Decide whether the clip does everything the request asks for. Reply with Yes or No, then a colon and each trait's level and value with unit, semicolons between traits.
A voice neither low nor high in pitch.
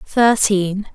No: high, 205 Hz